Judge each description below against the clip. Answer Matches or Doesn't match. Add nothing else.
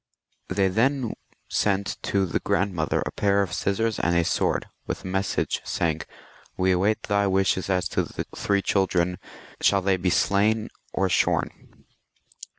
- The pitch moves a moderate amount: Doesn't match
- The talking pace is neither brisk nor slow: Matches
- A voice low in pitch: Matches